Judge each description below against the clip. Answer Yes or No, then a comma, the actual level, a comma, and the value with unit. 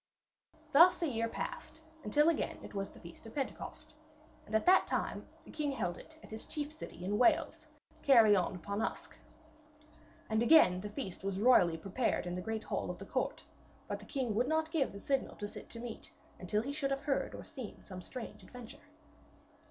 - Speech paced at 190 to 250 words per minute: Yes, average, 200 wpm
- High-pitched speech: Yes, high, 230 Hz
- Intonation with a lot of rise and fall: Yes, wide, 5.8 semitones